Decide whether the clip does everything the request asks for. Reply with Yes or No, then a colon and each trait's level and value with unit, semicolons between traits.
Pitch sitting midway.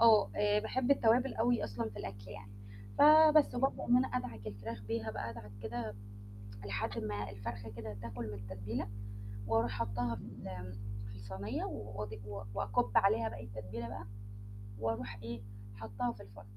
No: low, 110 Hz